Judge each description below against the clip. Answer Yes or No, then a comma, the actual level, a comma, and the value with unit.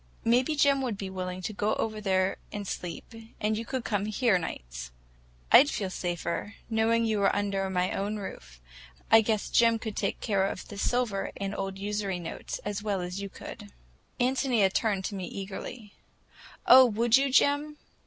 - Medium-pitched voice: No, high, 205 Hz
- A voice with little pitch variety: No, average, 3.2 semitones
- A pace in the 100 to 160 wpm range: No, average, 180 wpm